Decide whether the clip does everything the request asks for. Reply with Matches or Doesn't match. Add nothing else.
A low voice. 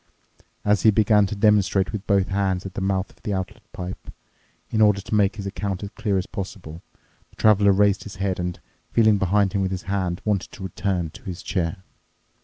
Matches